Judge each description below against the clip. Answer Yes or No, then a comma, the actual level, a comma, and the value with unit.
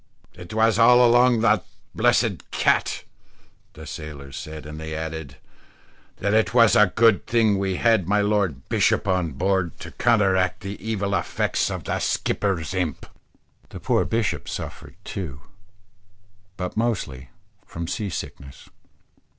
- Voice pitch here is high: No, very low, 95 Hz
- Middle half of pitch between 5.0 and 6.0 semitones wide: Yes, wide, 5.5 semitones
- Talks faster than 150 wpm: No, average, 140 wpm